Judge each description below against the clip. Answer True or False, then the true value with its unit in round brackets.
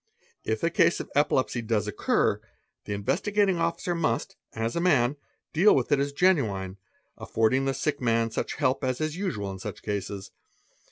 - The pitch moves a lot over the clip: True (7.2 semitones)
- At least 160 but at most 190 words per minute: True (175 wpm)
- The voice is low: True (130 Hz)